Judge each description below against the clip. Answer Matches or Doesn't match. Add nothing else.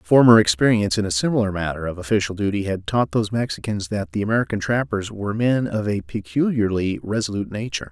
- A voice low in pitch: Matches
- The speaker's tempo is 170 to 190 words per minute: Matches